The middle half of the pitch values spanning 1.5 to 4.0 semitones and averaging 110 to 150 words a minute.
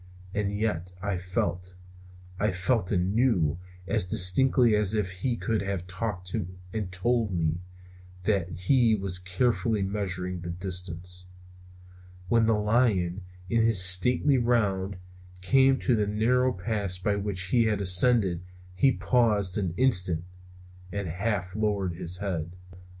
Yes: average, 3.7 semitones; slow, 135 wpm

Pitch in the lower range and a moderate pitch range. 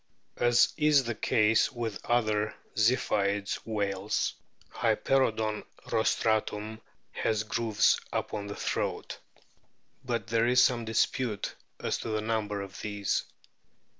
No: low, 110 Hz; narrow, 2.0 semitones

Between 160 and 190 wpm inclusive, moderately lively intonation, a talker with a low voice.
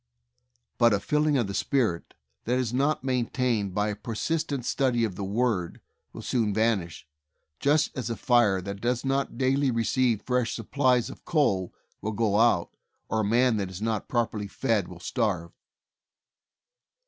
Yes: average, 165 wpm; average, 3.9 semitones; low, 115 Hz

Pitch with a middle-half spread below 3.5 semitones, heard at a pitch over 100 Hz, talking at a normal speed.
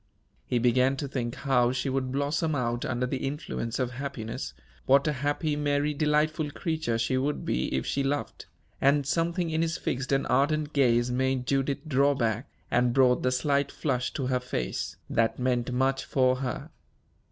Yes: narrow, 2.5 semitones; low, 135 Hz; average, 175 wpm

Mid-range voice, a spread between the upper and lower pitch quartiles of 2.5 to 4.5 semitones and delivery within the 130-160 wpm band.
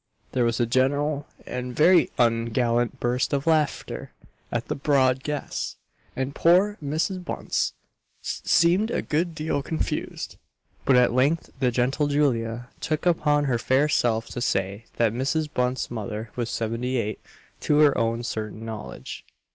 No: low, 130 Hz; average, 4.2 semitones; average, 145 wpm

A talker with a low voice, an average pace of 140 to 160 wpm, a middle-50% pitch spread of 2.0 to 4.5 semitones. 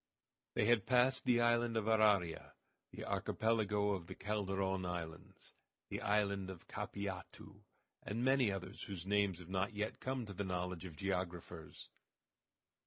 Yes: low, 100 Hz; average, 145 wpm; average, 3.0 semitones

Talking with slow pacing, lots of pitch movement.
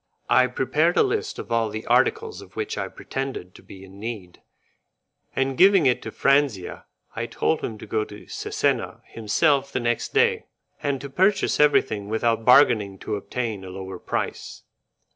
No: average, 170 wpm; wide, 6.4 semitones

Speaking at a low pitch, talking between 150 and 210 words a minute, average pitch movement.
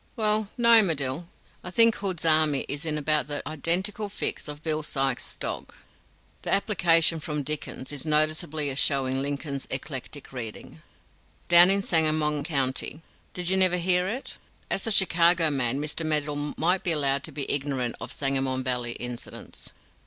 No: medium, 155 Hz; average, 160 wpm; average, 4.1 semitones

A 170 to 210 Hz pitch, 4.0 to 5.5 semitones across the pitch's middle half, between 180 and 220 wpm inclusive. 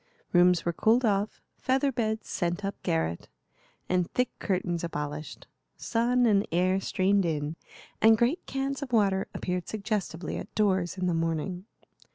No: high, 190 Hz; average, 4.3 semitones; average, 150 wpm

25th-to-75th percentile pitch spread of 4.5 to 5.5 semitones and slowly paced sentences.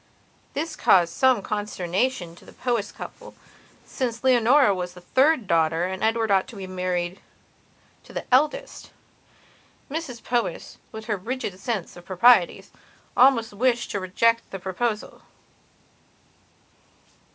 Yes: average, 5.0 semitones; slow, 130 wpm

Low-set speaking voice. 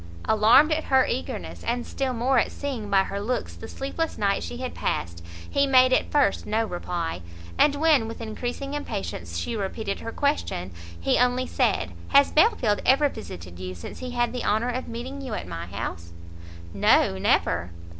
No: high, 230 Hz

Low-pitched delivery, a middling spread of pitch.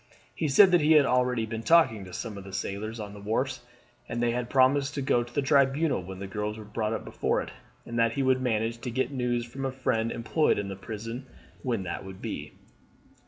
Yes: low, 120 Hz; average, 3.7 semitones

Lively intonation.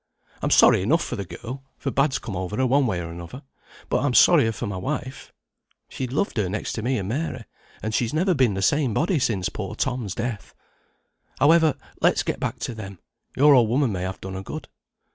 Yes: wide, 5.8 semitones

